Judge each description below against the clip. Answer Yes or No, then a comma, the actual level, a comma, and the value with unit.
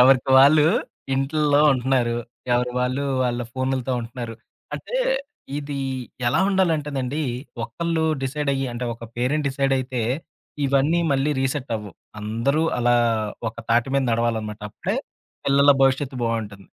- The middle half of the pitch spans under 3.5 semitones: Yes, average, 2.9 semitones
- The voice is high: No, low, 130 Hz